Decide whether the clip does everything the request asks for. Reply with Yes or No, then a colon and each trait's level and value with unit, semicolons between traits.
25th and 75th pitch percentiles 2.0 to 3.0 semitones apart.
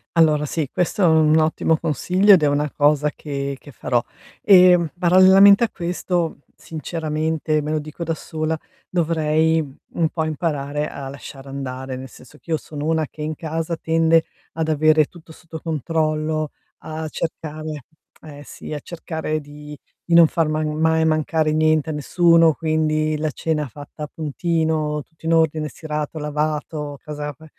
No: narrow, 1.5 semitones